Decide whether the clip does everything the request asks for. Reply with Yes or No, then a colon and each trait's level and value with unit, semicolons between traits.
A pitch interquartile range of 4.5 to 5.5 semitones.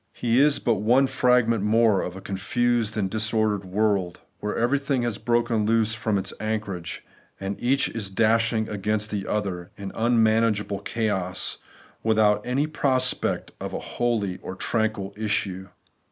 No: average, 2.7 semitones